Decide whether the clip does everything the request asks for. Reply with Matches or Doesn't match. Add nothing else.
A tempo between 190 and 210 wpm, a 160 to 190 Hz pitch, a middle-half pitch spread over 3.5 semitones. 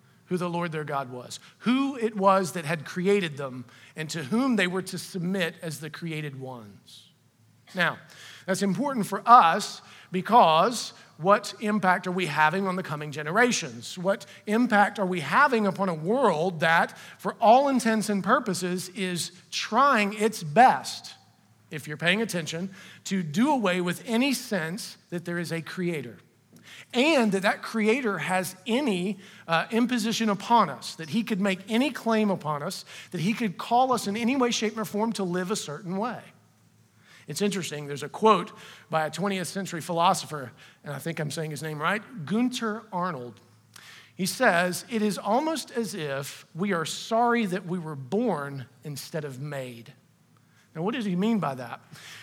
Doesn't match